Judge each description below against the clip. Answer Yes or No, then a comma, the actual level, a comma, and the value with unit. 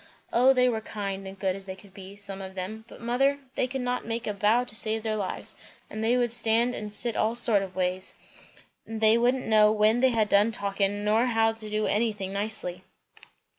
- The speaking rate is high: Yes, fast, 220 wpm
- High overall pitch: Yes, high, 215 Hz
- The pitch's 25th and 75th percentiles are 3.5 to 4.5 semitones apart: No, average, 2.8 semitones